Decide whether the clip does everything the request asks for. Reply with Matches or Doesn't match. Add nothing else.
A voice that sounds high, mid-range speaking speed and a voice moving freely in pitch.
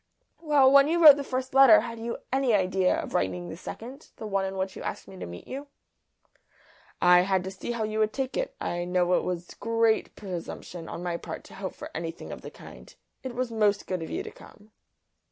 Doesn't match